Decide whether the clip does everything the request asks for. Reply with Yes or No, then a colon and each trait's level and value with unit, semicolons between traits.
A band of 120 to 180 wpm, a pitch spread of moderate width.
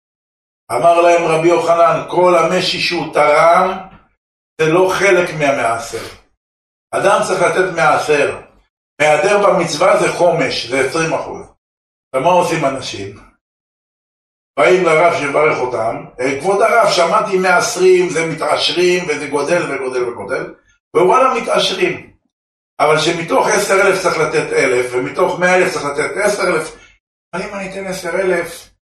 Yes: average, 125 wpm; average, 3.8 semitones